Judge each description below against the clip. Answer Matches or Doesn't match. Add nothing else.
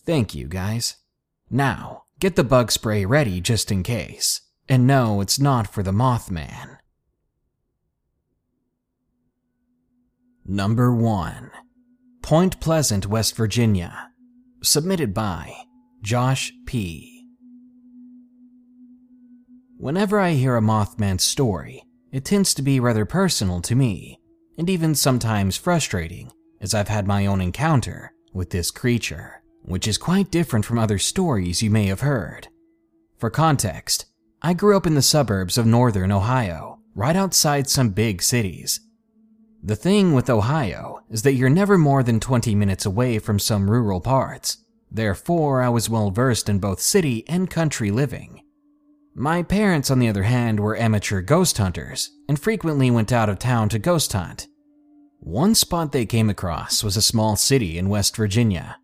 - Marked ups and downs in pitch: Matches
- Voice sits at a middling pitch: Doesn't match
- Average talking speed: Matches